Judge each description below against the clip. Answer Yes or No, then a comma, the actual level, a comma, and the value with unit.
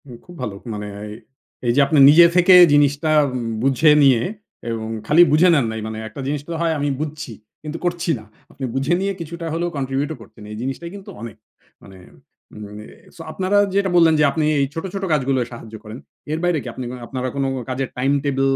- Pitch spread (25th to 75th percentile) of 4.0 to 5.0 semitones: Yes, average, 4.7 semitones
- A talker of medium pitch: Yes, medium, 145 Hz